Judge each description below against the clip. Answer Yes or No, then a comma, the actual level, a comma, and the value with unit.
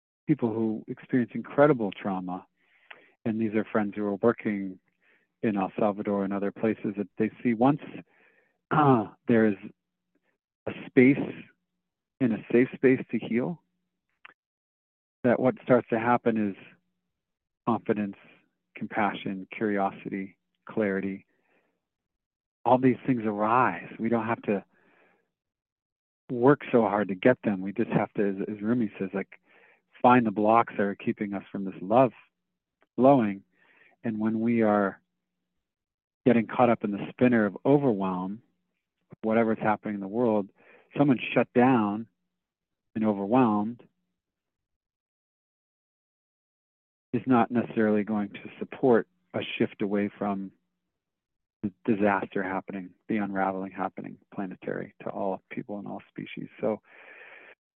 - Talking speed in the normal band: No, slow, 130 wpm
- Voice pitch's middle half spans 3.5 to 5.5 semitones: No, average, 3.1 semitones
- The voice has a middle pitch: No, low, 110 Hz